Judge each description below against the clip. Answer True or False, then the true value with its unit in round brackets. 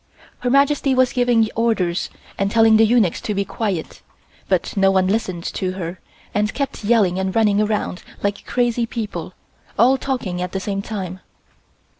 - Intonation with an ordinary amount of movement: True (3.8 semitones)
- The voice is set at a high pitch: True (210 Hz)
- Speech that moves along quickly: False (165 wpm)